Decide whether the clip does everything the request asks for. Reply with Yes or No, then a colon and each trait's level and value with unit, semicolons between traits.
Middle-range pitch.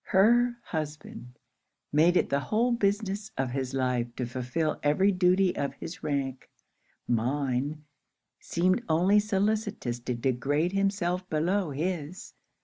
Yes: medium, 160 Hz